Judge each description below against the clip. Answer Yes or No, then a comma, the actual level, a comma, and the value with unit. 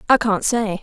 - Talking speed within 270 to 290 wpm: No, fast, 215 wpm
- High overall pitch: Yes, high, 220 Hz